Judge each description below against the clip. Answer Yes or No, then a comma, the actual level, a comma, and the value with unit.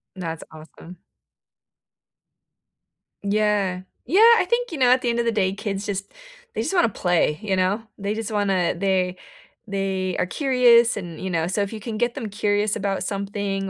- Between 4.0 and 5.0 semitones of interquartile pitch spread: No, average, 3.1 semitones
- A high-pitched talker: Yes, high, 200 Hz